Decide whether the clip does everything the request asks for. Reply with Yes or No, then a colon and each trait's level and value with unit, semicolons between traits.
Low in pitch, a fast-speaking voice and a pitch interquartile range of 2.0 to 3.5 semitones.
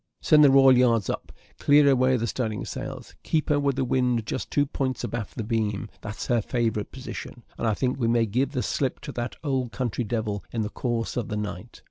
Yes: low, 125 Hz; fast, 220 wpm; average, 2.8 semitones